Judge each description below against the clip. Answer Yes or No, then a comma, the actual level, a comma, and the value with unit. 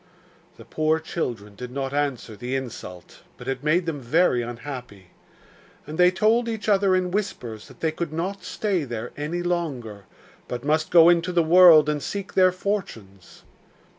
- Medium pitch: Yes, medium, 155 Hz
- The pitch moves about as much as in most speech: No, wide, 6.5 semitones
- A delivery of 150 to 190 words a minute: Yes, average, 165 wpm